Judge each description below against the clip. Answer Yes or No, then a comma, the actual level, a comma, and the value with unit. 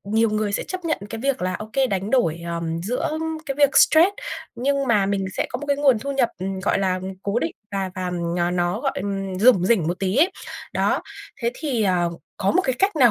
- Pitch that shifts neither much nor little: No, wide, 6.4 semitones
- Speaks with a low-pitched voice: No, high, 215 Hz